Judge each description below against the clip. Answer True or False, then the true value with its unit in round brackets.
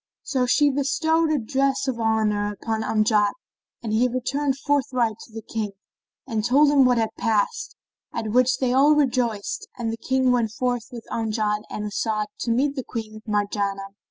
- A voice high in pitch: True (235 Hz)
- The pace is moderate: True (170 wpm)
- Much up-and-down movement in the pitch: False (3.6 semitones)